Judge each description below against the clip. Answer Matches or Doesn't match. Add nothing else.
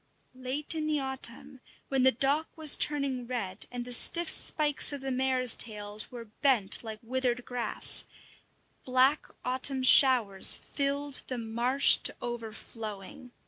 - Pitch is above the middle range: Matches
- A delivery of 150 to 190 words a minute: Doesn't match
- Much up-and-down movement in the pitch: Doesn't match